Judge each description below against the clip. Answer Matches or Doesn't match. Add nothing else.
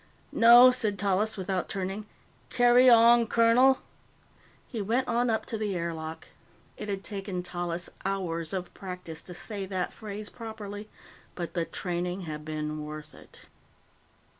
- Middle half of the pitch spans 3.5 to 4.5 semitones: Matches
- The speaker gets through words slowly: Doesn't match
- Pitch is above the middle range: Matches